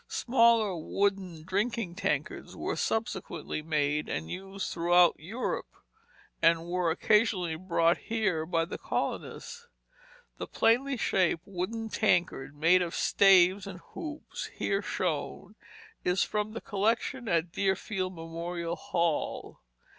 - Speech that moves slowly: Yes, slow, 120 wpm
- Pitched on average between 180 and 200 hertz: Yes, medium, 185 Hz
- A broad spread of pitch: No, average, 4.0 semitones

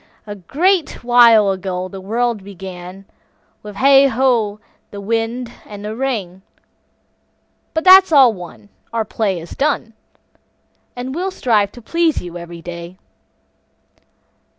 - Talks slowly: Yes, slow, 130 wpm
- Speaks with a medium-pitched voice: No, high, 220 Hz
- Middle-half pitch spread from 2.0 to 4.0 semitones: No, average, 5.2 semitones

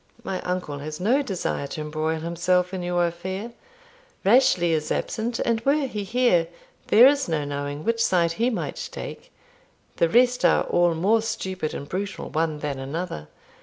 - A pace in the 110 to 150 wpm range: No, average, 165 wpm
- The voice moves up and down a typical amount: No, wide, 6.0 semitones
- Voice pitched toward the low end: No, medium, 180 Hz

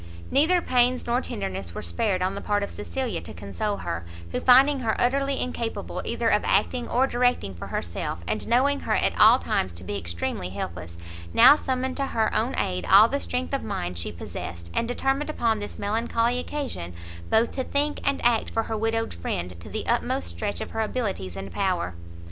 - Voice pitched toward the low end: No, high, 220 Hz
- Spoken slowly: No, average, 195 wpm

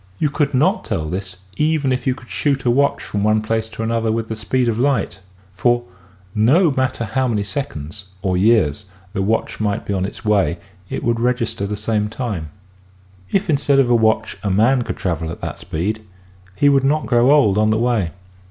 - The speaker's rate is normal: No, fast, 215 wpm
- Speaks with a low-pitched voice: Yes, low, 115 Hz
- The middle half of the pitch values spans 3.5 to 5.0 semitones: Yes, average, 4.4 semitones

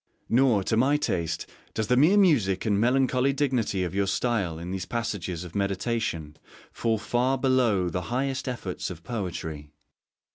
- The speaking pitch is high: No, low, 110 Hz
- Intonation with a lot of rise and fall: Yes, wide, 5.8 semitones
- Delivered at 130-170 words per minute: Yes, average, 155 wpm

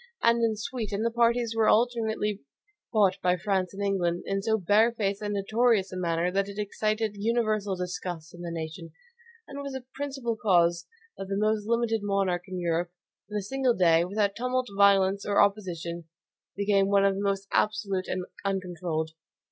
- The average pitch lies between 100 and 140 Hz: No, high, 200 Hz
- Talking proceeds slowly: No, average, 170 wpm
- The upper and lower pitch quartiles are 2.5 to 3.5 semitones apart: Yes, average, 3.2 semitones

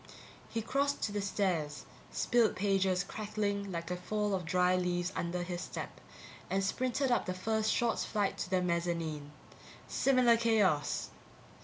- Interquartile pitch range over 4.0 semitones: No, average, 3.5 semitones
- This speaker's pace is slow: No, average, 155 wpm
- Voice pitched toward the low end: No, high, 195 Hz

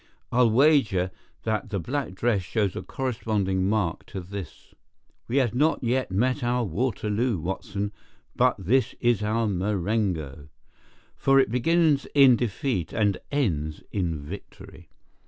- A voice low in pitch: Yes, low, 110 Hz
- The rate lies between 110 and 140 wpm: Yes, slow, 135 wpm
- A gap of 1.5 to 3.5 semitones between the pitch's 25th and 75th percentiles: No, average, 5.0 semitones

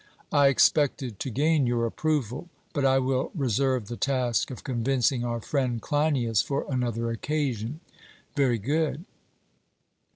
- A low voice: Yes, low, 130 Hz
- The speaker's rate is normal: No, slow, 130 wpm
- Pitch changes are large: No, average, 3.3 semitones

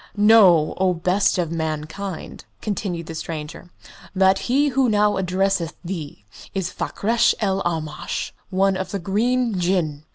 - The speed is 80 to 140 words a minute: Yes, slow, 135 wpm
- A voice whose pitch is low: No, high, 190 Hz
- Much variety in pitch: No, average, 3.5 semitones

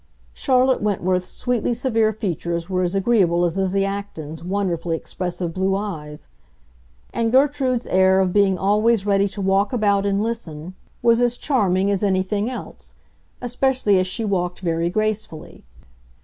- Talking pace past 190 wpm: No, average, 145 wpm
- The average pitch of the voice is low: No, high, 195 Hz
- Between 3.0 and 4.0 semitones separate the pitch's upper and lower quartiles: Yes, average, 3.6 semitones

